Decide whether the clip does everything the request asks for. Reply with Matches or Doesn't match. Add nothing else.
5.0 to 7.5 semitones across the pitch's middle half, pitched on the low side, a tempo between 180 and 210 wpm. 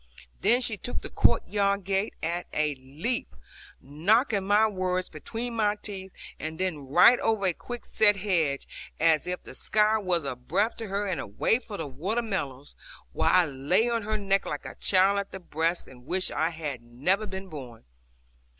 Doesn't match